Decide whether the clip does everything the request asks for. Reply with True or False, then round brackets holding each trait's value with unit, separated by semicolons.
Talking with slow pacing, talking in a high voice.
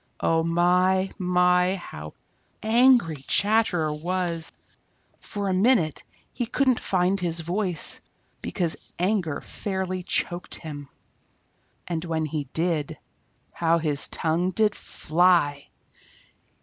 False (110 wpm; 180 Hz)